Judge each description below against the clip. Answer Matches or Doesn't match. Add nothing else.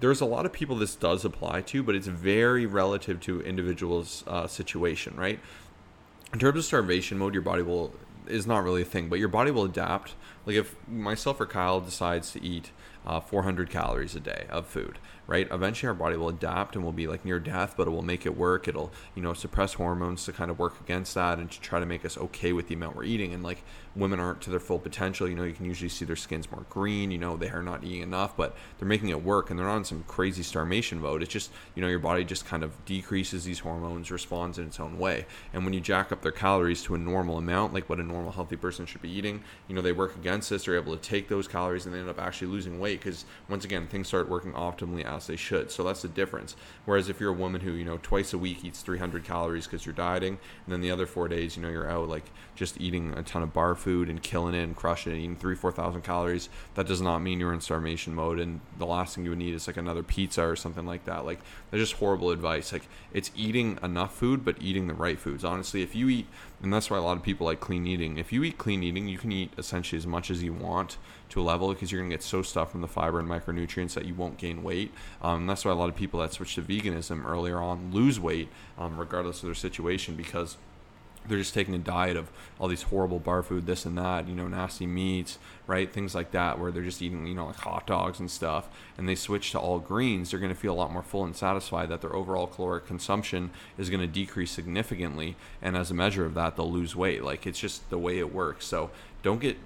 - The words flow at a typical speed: Doesn't match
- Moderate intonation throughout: Doesn't match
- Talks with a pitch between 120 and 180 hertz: Doesn't match